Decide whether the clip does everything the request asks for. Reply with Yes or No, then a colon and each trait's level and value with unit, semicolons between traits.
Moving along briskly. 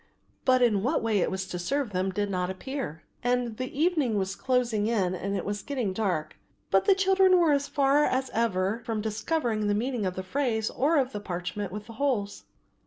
Yes: fast, 210 wpm